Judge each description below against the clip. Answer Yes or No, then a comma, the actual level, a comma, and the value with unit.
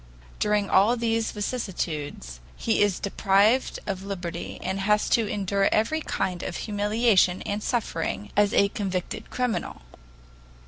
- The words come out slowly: Yes, slow, 130 wpm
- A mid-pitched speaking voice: No, high, 205 Hz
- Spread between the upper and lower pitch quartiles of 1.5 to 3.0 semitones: Yes, narrow, 2.5 semitones